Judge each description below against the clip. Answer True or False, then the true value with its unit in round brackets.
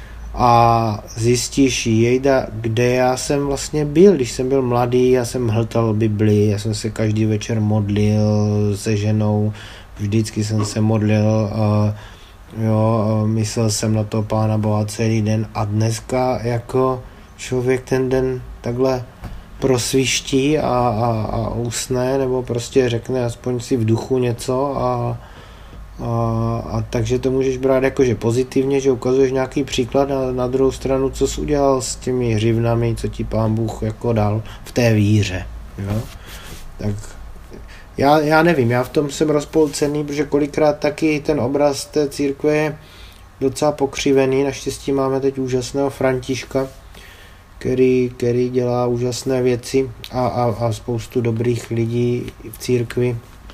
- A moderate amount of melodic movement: True (3.4 semitones)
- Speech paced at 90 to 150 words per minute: True (145 wpm)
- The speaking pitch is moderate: False (120 Hz)